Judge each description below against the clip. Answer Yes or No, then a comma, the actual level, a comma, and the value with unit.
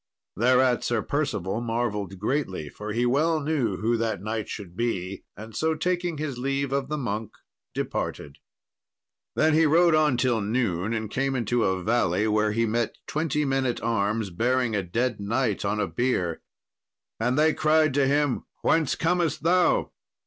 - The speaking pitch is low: Yes, low, 120 Hz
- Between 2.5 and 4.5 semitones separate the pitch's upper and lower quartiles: No, average, 5.3 semitones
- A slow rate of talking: No, average, 165 wpm